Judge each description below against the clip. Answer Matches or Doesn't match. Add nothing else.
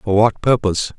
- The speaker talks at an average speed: Matches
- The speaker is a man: Matches